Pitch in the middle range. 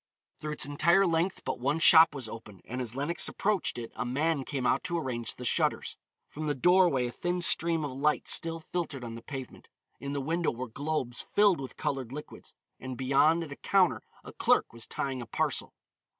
Yes: medium, 145 Hz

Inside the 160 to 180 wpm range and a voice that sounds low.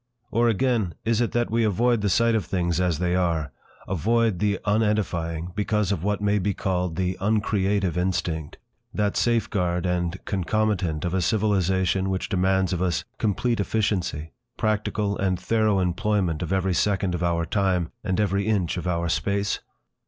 Yes: average, 165 wpm; very low, 95 Hz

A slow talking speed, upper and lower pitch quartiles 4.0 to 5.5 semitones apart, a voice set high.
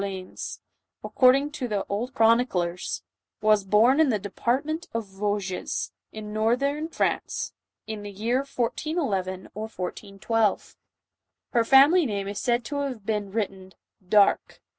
Yes: slow, 130 wpm; average, 4.3 semitones; high, 220 Hz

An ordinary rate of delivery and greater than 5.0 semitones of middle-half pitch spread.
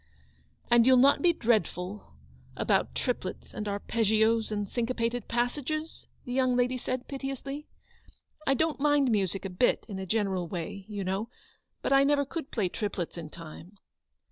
Yes: average, 160 wpm; wide, 5.4 semitones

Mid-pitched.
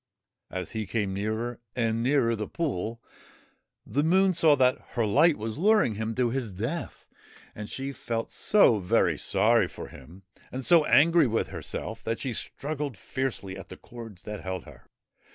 No: low, 115 Hz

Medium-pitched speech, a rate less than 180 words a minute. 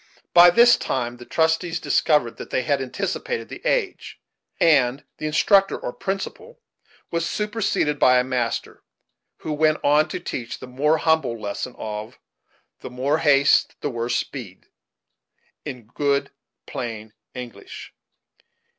Yes: medium, 145 Hz; slow, 135 wpm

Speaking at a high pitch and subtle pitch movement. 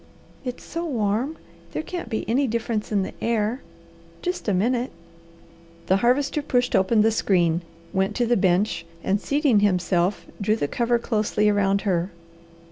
No: high, 215 Hz; average, 4.0 semitones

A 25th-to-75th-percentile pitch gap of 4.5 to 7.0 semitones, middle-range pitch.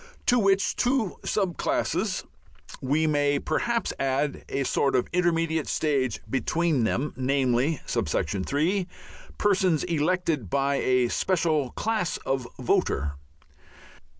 Yes: average, 5.1 semitones; medium, 150 Hz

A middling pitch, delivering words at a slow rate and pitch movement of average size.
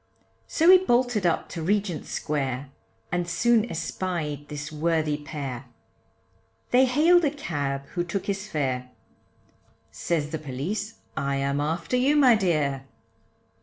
No: medium, 165 Hz; slow, 130 wpm; wide, 6.7 semitones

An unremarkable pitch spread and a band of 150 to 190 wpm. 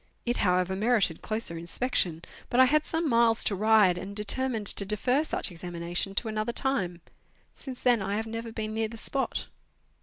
Yes: average, 4.3 semitones; average, 180 wpm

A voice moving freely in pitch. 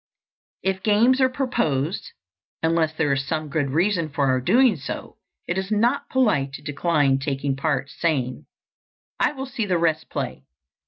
Yes: wide, 7.0 semitones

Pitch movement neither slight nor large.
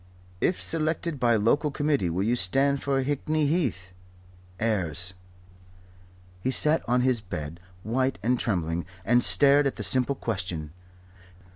No: wide, 7.2 semitones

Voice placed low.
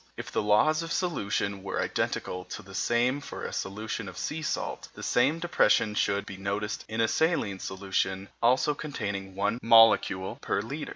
Yes: low, 105 Hz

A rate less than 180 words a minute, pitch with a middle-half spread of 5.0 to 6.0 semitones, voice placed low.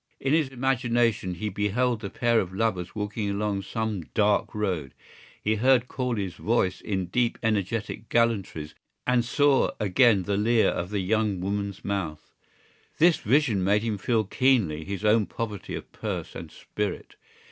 No: average, 155 wpm; average, 3.3 semitones; low, 105 Hz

